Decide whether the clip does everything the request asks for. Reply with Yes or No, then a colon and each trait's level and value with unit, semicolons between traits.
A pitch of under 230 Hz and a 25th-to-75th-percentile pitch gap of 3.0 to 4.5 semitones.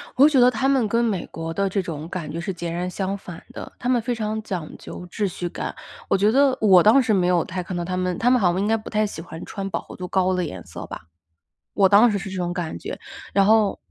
Yes: high, 195 Hz; average, 3.6 semitones